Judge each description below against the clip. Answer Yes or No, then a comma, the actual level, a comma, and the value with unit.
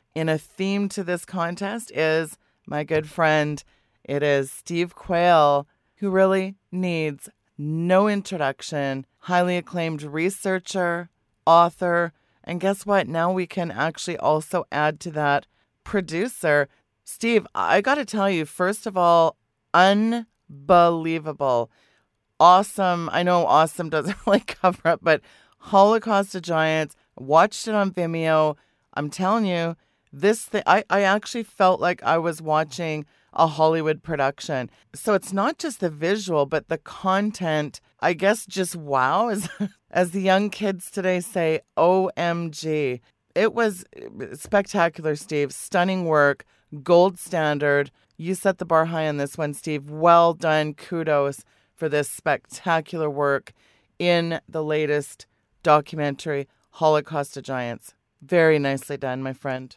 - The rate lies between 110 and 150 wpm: Yes, slow, 135 wpm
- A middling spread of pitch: Yes, average, 4.0 semitones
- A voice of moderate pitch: Yes, medium, 165 Hz